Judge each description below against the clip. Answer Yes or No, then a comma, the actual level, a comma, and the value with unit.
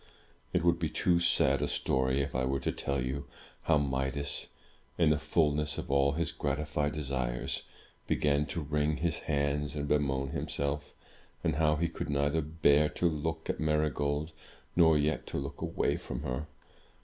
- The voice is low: Yes, very low, 75 Hz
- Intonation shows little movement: Yes, narrow, 1.7 semitones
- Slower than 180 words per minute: Yes, average, 170 wpm